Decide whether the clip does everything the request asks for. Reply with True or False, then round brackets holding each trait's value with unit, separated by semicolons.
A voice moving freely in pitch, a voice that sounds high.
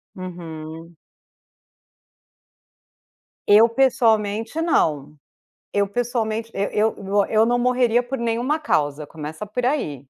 True (6.5 semitones; 220 Hz)